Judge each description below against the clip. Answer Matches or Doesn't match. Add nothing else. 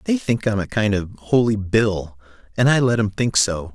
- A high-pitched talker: Doesn't match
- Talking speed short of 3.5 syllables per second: Doesn't match